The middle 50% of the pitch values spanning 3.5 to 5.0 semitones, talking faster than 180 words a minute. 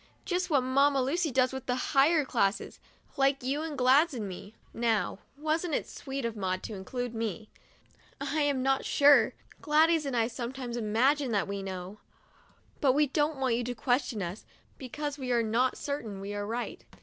Yes: average, 4.2 semitones; average, 195 wpm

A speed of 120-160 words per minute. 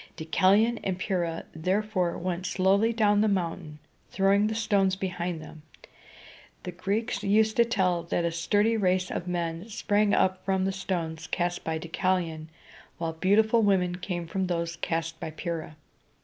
Yes: average, 155 wpm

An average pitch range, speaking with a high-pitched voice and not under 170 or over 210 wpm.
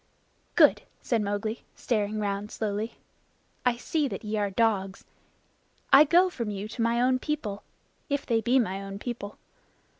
No: average, 3.5 semitones; high, 220 Hz; average, 155 wpm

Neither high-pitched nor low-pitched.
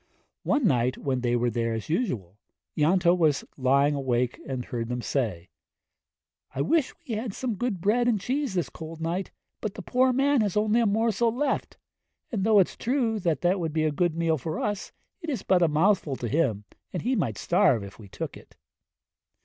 Yes: medium, 170 Hz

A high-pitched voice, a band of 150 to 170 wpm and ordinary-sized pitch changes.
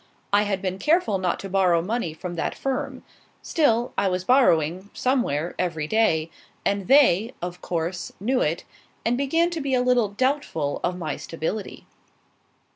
No: high, 195 Hz; average, 160 wpm; wide, 6.5 semitones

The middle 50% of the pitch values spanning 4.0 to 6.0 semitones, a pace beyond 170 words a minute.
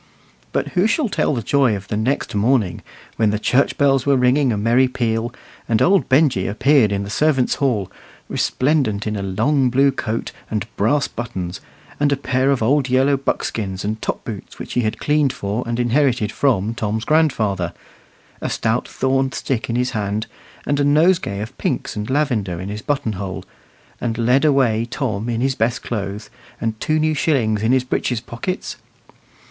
Yes: average, 4.3 semitones; average, 180 wpm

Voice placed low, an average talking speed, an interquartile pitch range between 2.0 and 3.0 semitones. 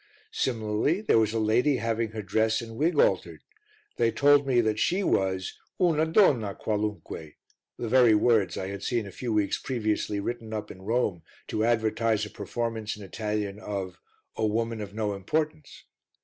Yes: low, 110 Hz; average, 165 wpm; narrow, 2.5 semitones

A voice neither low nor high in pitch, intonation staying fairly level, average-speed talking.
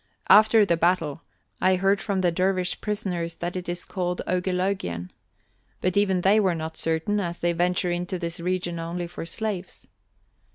Yes: medium, 180 Hz; narrow, 1.9 semitones; average, 165 wpm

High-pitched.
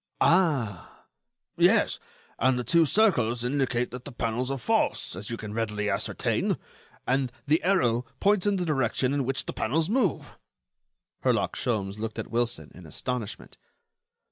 No: low, 125 Hz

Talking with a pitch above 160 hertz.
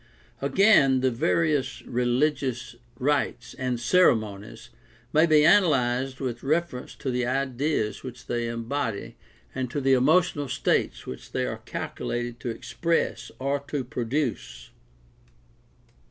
No: low, 130 Hz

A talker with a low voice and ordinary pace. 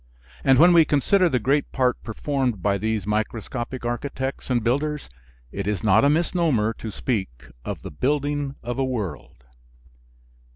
Yes: low, 125 Hz; average, 155 wpm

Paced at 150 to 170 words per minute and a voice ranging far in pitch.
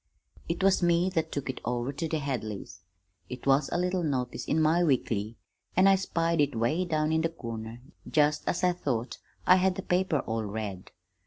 No: average, 195 wpm; wide, 6.3 semitones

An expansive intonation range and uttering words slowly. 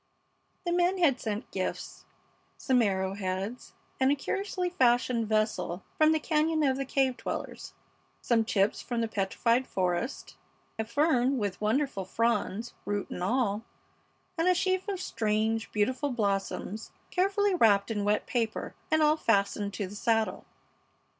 No: wide, 6.0 semitones; average, 145 wpm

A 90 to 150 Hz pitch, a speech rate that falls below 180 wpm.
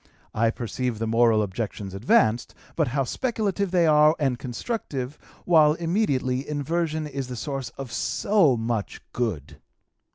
Yes: low, 135 Hz; slow, 135 wpm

